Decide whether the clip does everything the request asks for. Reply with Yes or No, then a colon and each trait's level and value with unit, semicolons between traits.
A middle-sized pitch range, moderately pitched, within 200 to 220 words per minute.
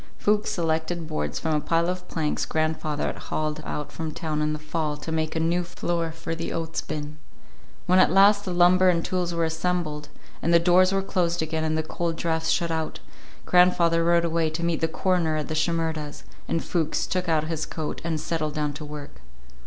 No: narrow, 1.9 semitones; medium, 165 Hz; fast, 205 wpm